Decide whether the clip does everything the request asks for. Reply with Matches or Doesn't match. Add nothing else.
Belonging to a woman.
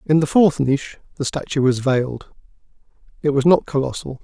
Doesn't match